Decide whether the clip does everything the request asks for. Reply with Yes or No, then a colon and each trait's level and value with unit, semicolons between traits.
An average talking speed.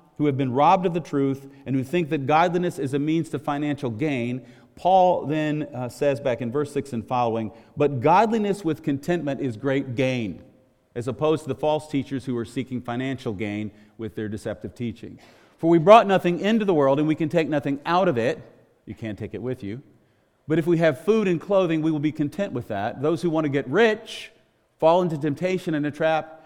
No: fast, 220 wpm